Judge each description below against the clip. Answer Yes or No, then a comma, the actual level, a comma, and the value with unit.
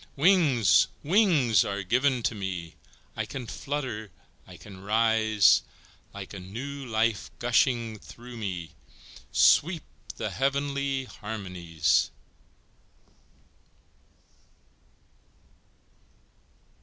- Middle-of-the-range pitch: No, low, 115 Hz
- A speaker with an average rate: No, slow, 80 wpm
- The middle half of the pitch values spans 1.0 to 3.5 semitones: No, wide, 5.6 semitones